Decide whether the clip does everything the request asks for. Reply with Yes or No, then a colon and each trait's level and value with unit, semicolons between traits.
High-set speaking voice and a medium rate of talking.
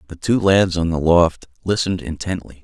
No: very low, 90 Hz; average, 180 wpm